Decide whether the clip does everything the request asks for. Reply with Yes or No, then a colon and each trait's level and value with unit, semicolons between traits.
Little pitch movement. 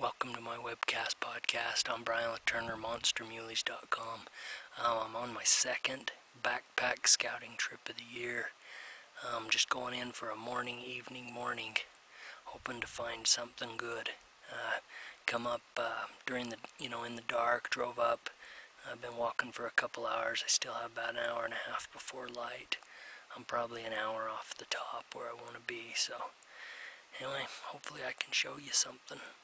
Yes: narrow, 1.1 semitones